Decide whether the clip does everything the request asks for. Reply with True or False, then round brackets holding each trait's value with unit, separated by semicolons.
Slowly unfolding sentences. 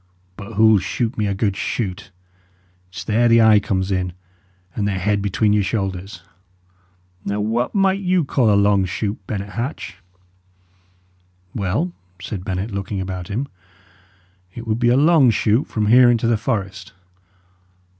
False (155 wpm)